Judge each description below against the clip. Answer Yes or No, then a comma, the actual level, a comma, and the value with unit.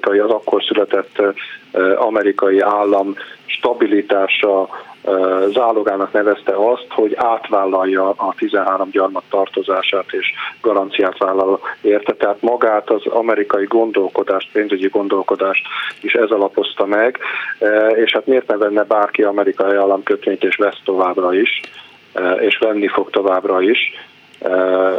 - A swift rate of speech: No, average, 120 wpm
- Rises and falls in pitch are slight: Yes, narrow, 1.4 semitones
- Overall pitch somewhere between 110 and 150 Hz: No, low, 100 Hz